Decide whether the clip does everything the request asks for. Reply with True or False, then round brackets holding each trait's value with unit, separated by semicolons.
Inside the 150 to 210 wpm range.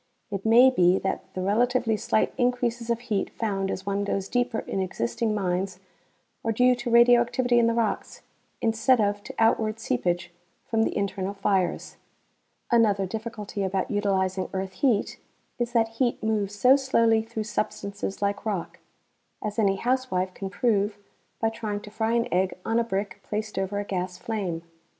True (165 wpm)